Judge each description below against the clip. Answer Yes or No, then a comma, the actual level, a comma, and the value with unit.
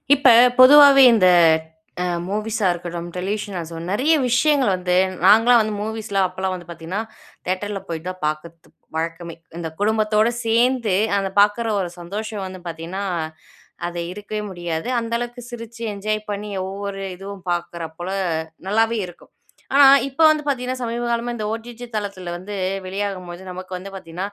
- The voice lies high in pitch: Yes, high, 205 Hz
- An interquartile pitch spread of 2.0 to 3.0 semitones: No, average, 4.1 semitones